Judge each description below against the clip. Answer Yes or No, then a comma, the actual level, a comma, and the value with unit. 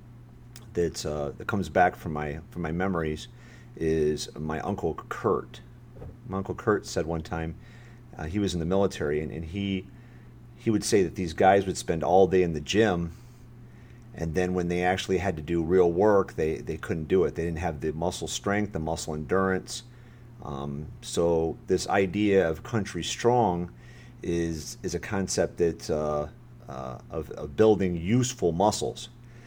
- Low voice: Yes, very low, 90 Hz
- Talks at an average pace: Yes, average, 175 wpm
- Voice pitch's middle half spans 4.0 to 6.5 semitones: Yes, average, 5.3 semitones